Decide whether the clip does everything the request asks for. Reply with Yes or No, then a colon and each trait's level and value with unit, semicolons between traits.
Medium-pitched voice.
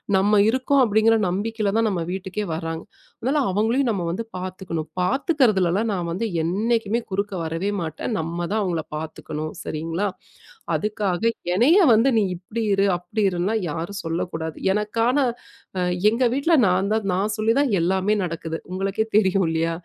No: high, 195 Hz